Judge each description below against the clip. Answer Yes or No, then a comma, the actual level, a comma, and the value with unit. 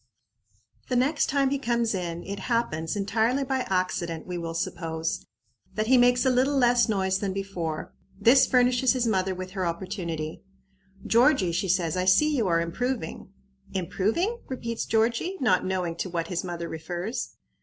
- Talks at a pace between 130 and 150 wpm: No, average, 165 wpm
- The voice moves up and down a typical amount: No, wide, 6.1 semitones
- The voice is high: Yes, high, 195 Hz